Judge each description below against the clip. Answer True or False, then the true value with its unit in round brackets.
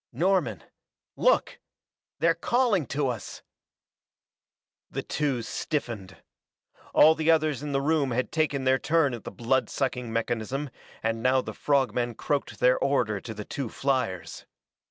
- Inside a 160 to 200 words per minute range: False (145 wpm)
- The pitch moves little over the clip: False (4.0 semitones)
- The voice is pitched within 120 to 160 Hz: True (135 Hz)